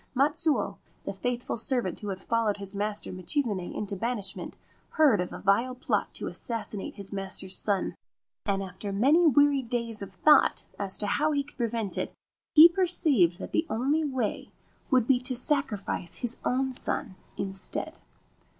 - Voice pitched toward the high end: Yes, high, 230 Hz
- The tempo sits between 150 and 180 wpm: Yes, average, 165 wpm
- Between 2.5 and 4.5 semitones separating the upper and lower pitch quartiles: No, wide, 5.4 semitones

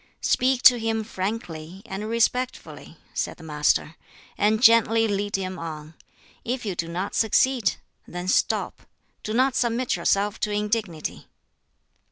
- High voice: Yes, high, 210 Hz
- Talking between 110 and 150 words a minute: Yes, slow, 135 wpm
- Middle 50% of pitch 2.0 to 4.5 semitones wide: Yes, average, 4.0 semitones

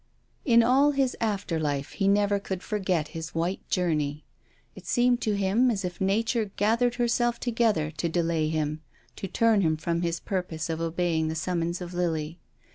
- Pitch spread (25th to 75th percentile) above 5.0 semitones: Yes, wide, 5.4 semitones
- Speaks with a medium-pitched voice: Yes, medium, 180 Hz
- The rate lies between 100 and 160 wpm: No, average, 175 wpm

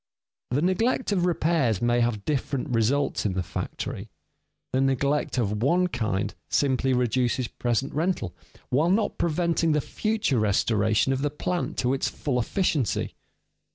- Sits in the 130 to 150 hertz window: Yes, low, 135 Hz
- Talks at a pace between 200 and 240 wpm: No, average, 150 wpm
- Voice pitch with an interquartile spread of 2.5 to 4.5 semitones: No, wide, 5.5 semitones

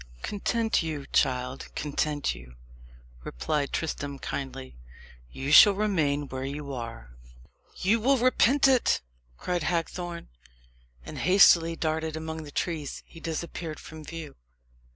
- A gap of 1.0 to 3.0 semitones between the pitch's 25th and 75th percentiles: No, average, 3.9 semitones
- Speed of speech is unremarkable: No, slow, 120 wpm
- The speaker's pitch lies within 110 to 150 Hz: No, medium, 160 Hz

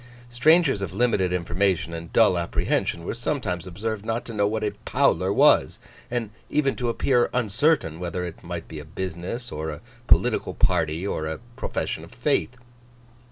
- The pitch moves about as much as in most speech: No, wide, 5.8 semitones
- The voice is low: Yes, low, 100 Hz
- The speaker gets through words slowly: No, average, 165 wpm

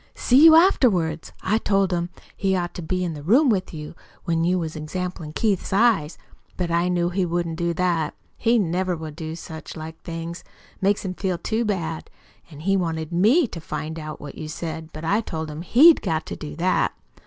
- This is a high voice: No, medium, 175 Hz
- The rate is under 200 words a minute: No, fast, 205 wpm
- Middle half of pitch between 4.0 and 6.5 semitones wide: No, average, 3.3 semitones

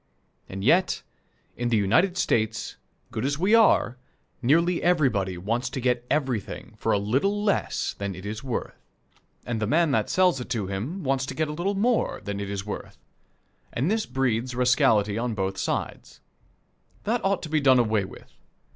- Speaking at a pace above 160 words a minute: Yes, average, 180 wpm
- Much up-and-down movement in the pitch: Yes, wide, 7.6 semitones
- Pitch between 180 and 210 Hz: No, low, 125 Hz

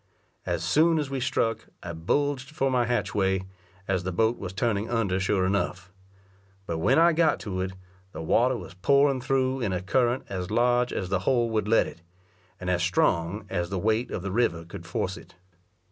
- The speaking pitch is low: Yes, low, 105 Hz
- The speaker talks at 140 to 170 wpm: No, average, 195 wpm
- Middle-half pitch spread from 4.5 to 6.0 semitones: Yes, wide, 5.4 semitones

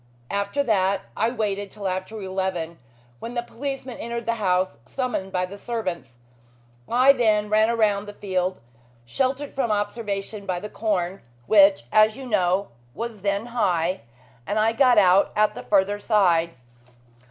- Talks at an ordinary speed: Yes, average, 155 wpm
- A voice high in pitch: Yes, high, 205 Hz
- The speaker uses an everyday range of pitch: Yes, average, 3.5 semitones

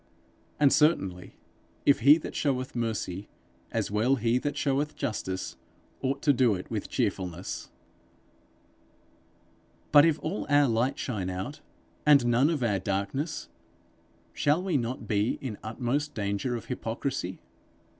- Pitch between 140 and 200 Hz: No, low, 125 Hz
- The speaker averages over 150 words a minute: No, slow, 135 wpm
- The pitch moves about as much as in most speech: No, wide, 5.8 semitones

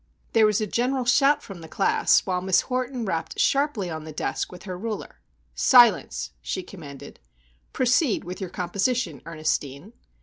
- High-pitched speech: Yes, high, 195 Hz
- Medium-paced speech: Yes, average, 160 wpm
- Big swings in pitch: Yes, wide, 6.6 semitones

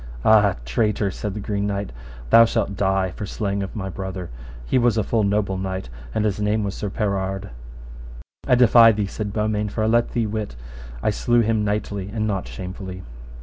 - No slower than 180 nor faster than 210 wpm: Yes, average, 190 wpm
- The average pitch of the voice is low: Yes, low, 105 Hz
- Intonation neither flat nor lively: No, narrow, 2.0 semitones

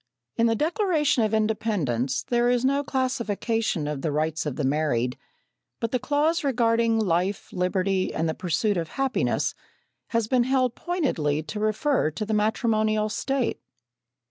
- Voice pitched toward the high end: Yes, high, 220 Hz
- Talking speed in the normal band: Yes, average, 150 wpm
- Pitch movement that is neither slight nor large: No, wide, 6.9 semitones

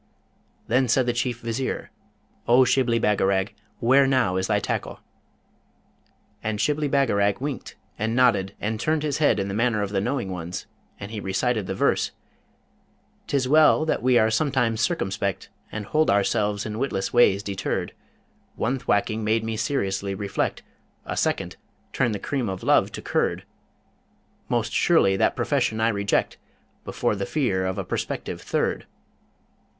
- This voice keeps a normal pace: Yes, average, 155 wpm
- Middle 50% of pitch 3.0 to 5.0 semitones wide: Yes, average, 4.3 semitones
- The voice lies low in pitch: Yes, low, 110 Hz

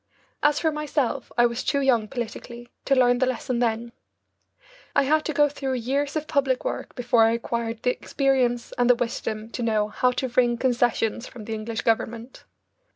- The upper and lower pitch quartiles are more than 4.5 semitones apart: No, narrow, 2.5 semitones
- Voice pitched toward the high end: Yes, high, 245 Hz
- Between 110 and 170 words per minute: No, average, 185 wpm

